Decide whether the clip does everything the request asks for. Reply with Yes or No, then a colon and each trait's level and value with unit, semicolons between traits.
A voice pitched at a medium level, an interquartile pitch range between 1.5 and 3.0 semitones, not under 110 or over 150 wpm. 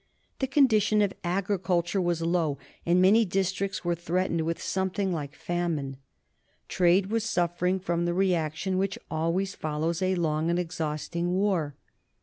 Yes: medium, 175 Hz; narrow, 2.4 semitones; average, 140 wpm